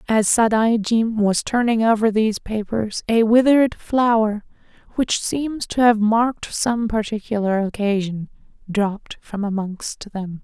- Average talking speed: No, slow, 125 wpm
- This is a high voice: Yes, high, 220 Hz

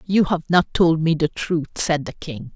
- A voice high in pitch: No, medium, 160 Hz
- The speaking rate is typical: No, fast, 235 wpm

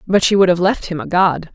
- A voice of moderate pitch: Yes, medium, 180 Hz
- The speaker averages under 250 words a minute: No, fast, 310 wpm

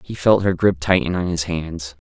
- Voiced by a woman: No, male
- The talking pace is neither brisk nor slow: No, fast, 230 wpm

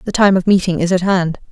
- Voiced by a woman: Yes, female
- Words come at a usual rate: No, fast, 275 wpm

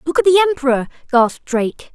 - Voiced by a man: No, female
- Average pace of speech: Yes, average, 185 wpm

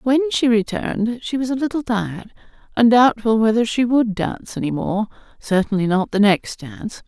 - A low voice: No, high, 225 Hz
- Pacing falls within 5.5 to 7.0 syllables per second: No, 5.2 syllables/s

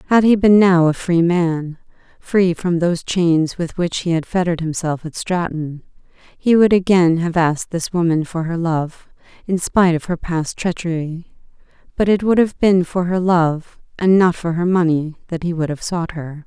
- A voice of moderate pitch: Yes, medium, 170 Hz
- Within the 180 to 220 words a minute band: Yes, average, 190 wpm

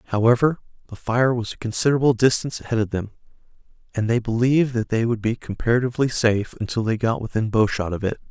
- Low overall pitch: Yes, low, 115 Hz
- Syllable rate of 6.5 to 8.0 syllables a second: Yes, 6.8 syllables/s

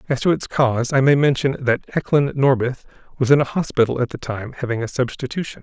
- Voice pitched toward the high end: No, low, 130 Hz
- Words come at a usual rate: No, fast, 215 wpm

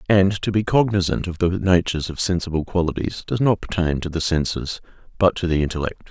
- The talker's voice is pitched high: No, very low, 90 Hz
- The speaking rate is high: No, average, 195 wpm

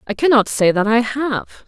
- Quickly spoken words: Yes, fast, 215 wpm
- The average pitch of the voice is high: Yes, high, 235 Hz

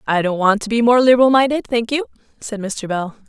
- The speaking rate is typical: No, fast, 240 wpm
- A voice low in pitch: No, high, 225 Hz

